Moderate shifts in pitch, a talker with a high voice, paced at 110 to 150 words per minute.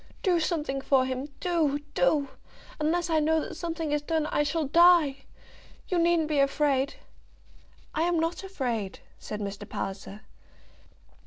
Yes: average, 3.6 semitones; very high, 300 Hz; average, 140 wpm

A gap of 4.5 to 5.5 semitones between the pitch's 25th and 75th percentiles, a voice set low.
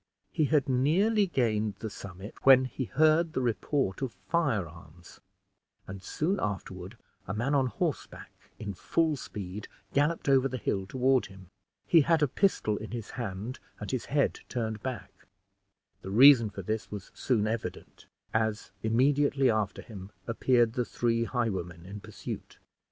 Yes: average, 5.0 semitones; low, 115 Hz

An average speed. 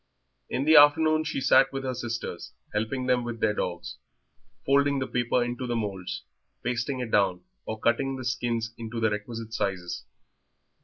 Yes: average, 165 wpm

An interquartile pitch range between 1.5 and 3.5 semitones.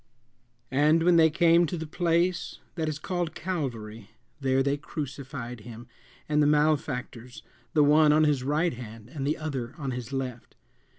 No: average, 3.9 semitones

